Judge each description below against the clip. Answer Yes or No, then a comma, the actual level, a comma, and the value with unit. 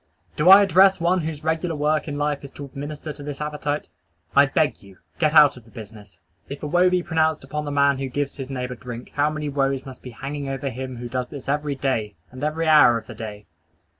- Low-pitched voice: No, medium, 145 Hz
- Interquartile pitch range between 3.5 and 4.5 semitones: No, average, 2.9 semitones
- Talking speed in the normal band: No, fast, 240 wpm